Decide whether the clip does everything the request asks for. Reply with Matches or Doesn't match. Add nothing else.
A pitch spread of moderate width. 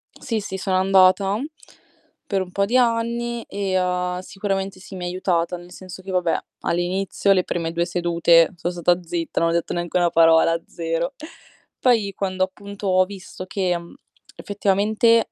Doesn't match